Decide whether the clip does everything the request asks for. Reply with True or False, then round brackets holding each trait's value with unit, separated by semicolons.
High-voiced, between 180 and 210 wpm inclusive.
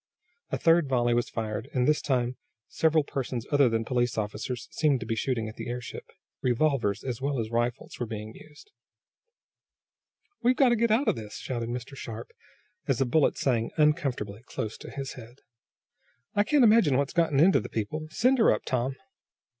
False (130 Hz; 185 wpm)